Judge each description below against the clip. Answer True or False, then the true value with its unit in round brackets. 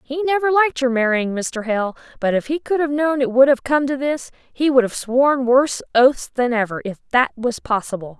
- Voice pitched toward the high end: True (260 Hz)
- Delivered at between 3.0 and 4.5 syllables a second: False (5.1 syllables/s)